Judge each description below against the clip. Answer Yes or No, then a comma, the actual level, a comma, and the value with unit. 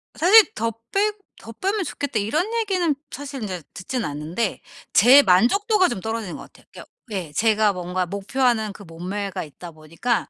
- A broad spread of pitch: Yes, wide, 7.8 semitones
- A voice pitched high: Yes, high, 220 Hz